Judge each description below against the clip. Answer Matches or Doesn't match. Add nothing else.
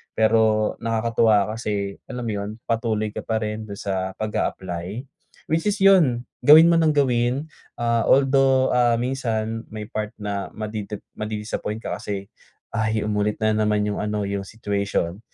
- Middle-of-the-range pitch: Doesn't match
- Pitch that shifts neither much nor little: Doesn't match